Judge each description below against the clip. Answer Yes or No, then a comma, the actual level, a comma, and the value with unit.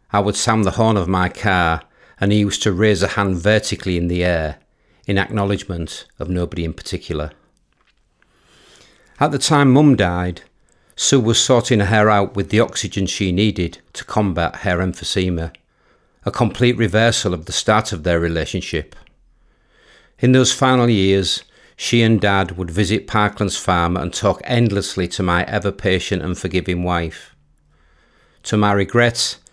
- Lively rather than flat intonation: No, average, 3.3 semitones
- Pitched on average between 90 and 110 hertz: Yes, very low, 95 Hz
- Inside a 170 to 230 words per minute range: No, average, 155 wpm